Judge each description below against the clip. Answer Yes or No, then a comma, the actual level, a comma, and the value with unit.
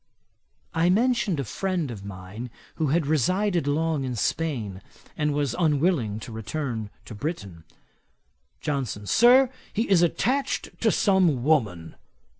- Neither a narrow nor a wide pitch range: No, wide, 7.9 semitones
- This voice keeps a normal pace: No, slow, 130 wpm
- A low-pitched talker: No, medium, 150 Hz